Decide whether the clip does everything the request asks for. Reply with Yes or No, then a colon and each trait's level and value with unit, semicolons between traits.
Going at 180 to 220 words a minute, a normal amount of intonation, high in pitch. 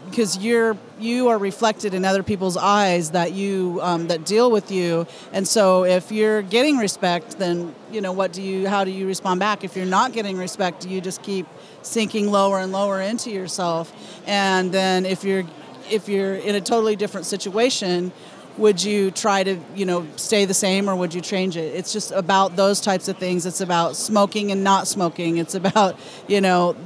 No: average, 200 wpm; narrow, 1.9 semitones; high, 195 Hz